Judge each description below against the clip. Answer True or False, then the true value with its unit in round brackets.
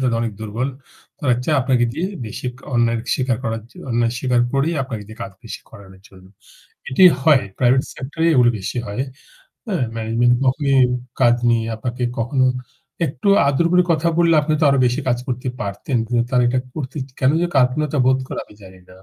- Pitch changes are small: False (3.1 semitones)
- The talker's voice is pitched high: False (125 Hz)